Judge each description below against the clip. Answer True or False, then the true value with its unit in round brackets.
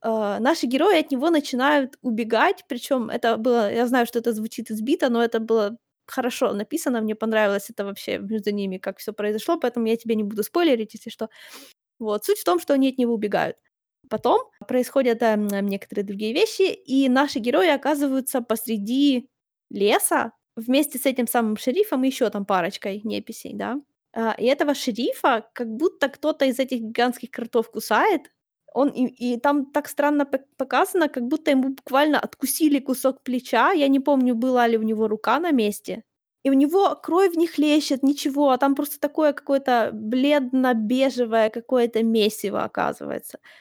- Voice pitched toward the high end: True (255 Hz)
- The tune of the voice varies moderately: True (4.2 semitones)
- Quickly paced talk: True (170 wpm)